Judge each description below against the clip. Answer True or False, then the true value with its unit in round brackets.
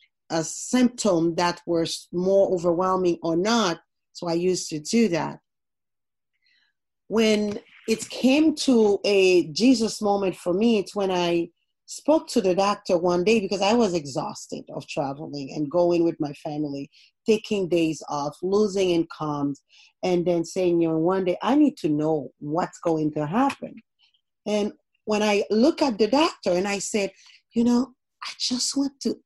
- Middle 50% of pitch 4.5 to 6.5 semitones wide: True (5.2 semitones)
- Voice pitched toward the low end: False (190 Hz)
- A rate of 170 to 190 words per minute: False (160 wpm)